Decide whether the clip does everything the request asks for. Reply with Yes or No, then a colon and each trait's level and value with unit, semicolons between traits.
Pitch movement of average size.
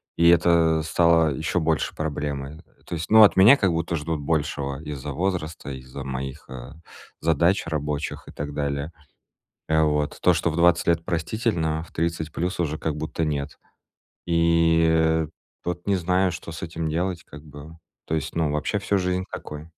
No: narrow, 2.3 semitones